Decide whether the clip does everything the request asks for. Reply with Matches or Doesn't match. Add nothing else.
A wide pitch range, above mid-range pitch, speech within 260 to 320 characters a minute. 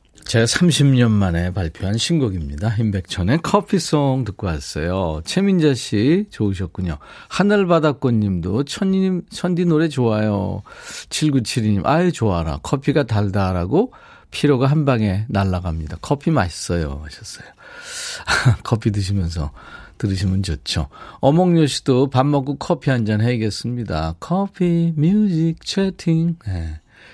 Doesn't match